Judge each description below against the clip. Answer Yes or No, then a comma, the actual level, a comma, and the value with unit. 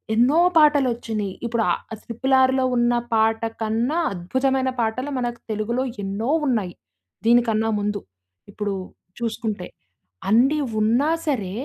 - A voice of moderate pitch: No, high, 235 Hz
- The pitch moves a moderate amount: Yes, average, 3.3 semitones